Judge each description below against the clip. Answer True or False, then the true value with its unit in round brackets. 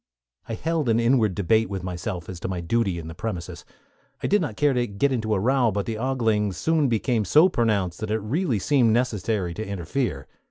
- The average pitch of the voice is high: False (110 Hz)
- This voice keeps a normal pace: False (210 wpm)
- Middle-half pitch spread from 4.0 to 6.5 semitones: True (4.7 semitones)